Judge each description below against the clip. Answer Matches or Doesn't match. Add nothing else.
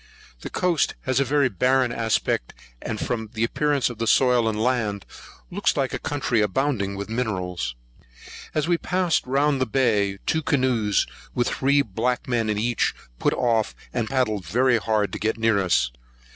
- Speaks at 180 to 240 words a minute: Doesn't match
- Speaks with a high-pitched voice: Doesn't match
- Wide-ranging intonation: Doesn't match